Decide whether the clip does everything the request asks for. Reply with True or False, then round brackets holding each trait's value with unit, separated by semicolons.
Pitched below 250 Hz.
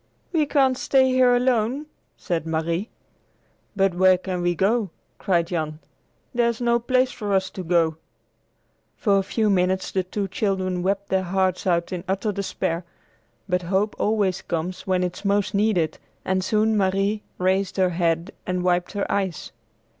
True (190 Hz)